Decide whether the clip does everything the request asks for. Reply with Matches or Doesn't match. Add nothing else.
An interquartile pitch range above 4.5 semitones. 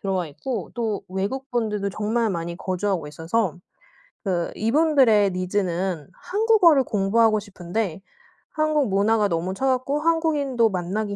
Matches